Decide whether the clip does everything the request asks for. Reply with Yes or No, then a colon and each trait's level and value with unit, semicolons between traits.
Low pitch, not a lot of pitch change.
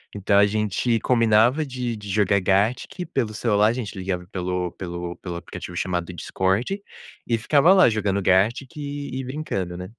No: low, 105 Hz; average, 5.0 semitones